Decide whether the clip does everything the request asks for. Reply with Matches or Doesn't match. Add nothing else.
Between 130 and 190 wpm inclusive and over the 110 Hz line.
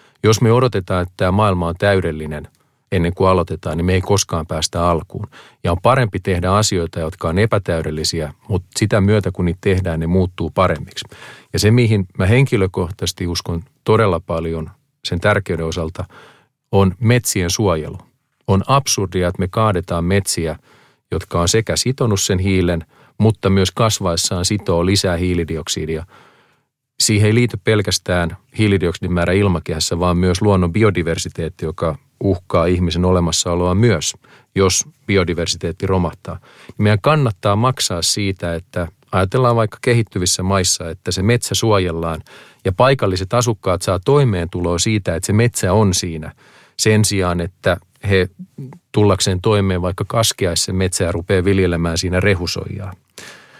Doesn't match